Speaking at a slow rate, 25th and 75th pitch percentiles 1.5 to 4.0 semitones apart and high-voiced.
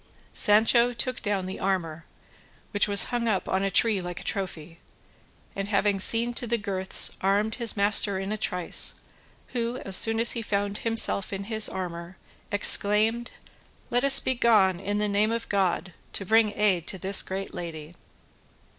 No: average, 170 wpm; average, 3.0 semitones; high, 205 Hz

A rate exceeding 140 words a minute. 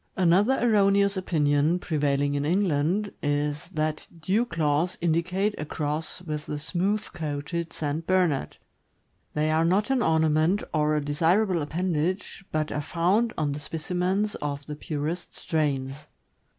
No: slow, 135 wpm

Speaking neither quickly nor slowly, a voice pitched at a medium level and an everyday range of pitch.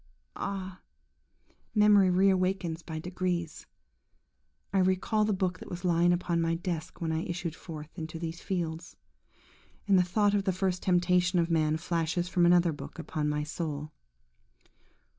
No: average, 155 wpm; medium, 175 Hz; narrow, 2.2 semitones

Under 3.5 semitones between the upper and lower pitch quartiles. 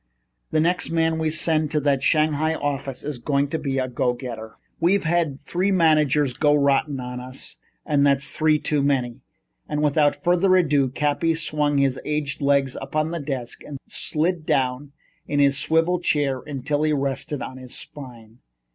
Yes: narrow, 2.5 semitones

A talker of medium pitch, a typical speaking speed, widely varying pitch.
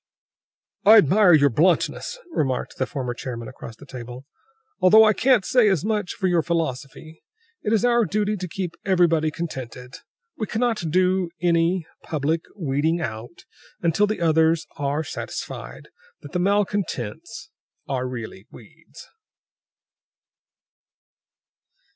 No: medium, 165 Hz; slow, 125 wpm; wide, 6.3 semitones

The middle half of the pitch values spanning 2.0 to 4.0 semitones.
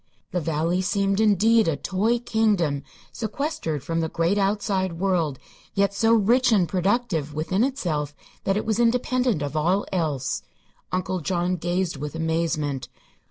No: average, 4.9 semitones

